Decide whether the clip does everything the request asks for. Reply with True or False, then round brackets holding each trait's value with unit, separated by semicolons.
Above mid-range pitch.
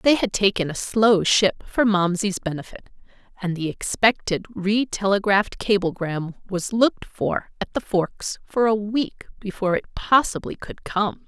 True (200 Hz)